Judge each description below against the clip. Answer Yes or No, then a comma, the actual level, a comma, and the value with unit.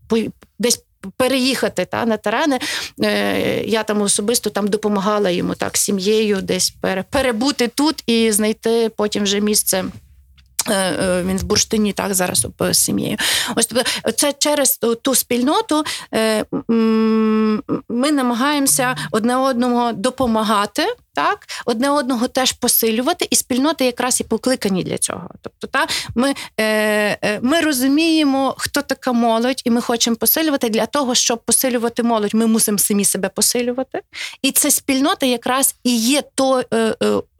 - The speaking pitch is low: No, high, 235 Hz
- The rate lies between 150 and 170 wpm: No, average, 125 wpm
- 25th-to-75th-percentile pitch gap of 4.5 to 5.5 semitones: No, average, 3.7 semitones